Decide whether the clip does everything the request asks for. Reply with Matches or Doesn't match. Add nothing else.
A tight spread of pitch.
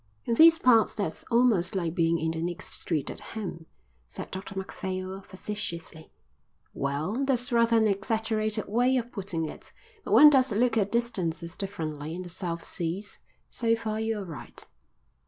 Doesn't match